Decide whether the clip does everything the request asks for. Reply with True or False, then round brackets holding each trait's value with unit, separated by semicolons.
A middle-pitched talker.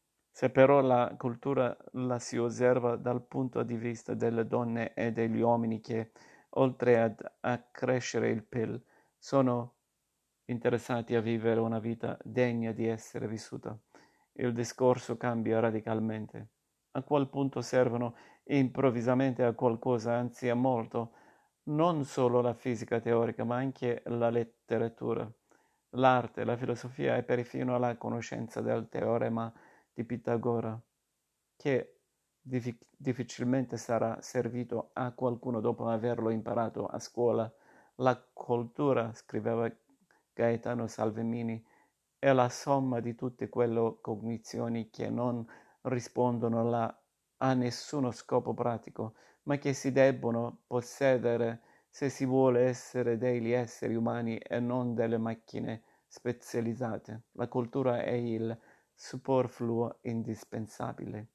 False (120 Hz)